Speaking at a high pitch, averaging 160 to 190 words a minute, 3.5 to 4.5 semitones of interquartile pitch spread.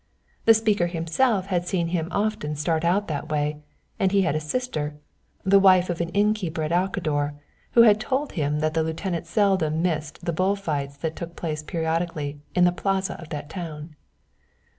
No: medium, 170 Hz; average, 185 wpm; average, 4.0 semitones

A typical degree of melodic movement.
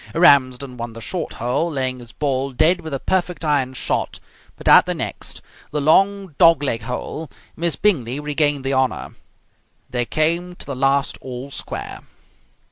Yes: average, 4.2 semitones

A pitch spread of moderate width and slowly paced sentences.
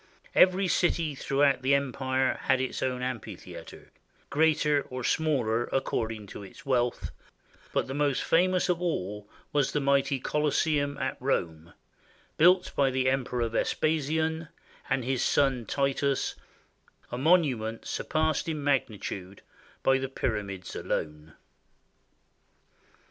Yes: average, 3.8 semitones; slow, 120 wpm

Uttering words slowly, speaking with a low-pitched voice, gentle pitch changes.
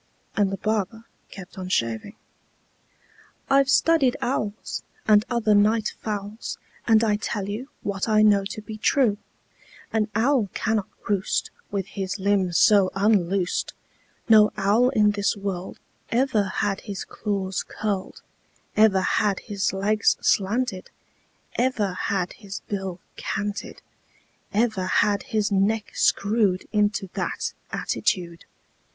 No: slow, 125 wpm; high, 205 Hz; narrow, 2.1 semitones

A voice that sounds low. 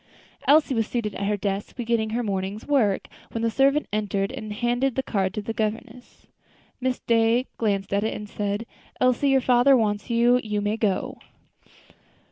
No: high, 225 Hz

